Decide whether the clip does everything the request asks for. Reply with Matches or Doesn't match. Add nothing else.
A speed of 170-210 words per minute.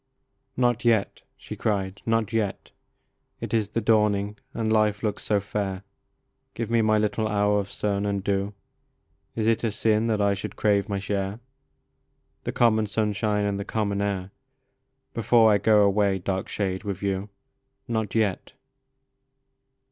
Doesn't match